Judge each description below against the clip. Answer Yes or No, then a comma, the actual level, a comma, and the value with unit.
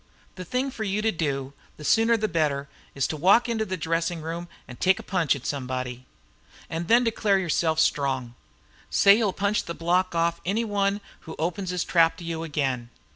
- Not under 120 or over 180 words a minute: No, average, 195 wpm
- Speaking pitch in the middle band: Yes, medium, 170 Hz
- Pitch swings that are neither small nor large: Yes, average, 4.9 semitones